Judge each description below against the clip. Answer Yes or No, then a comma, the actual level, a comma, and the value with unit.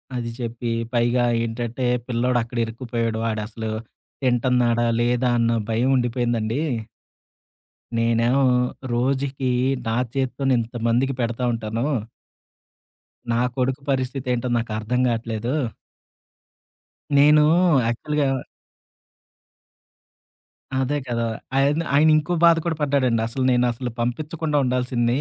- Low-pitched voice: Yes, low, 120 Hz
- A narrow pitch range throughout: Yes, narrow, 2.3 semitones